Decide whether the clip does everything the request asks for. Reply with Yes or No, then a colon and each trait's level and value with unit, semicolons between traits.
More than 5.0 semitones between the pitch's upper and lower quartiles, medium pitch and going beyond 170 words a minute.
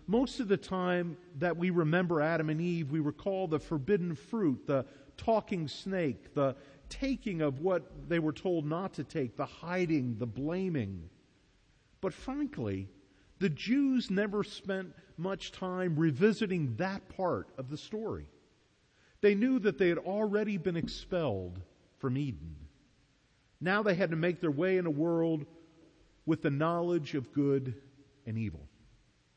No: wide, 5.4 semitones; medium, 165 Hz; average, 150 wpm